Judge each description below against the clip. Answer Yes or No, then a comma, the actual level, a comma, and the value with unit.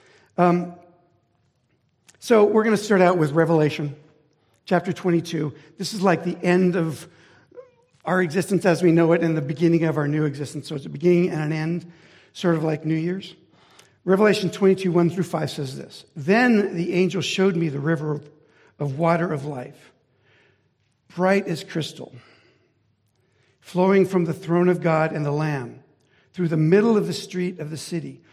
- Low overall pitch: No, medium, 170 Hz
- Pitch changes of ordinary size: Yes, average, 3.2 semitones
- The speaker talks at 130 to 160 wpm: No, average, 170 wpm